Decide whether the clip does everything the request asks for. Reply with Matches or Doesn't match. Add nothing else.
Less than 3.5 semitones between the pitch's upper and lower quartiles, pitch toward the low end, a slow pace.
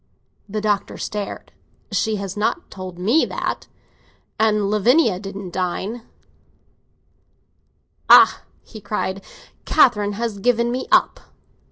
Doesn't match